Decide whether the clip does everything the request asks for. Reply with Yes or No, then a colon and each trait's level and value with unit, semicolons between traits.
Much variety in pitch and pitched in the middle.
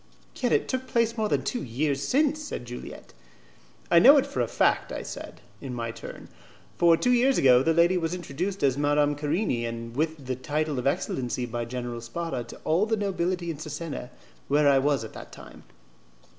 Yes: wide, 6.3 semitones; medium, 150 Hz